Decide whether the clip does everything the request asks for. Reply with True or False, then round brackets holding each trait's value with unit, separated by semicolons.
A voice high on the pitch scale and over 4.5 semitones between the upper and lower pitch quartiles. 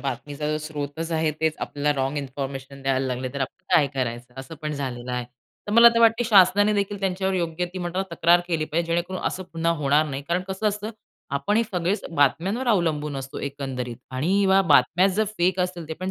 False (160 Hz; 5.2 semitones)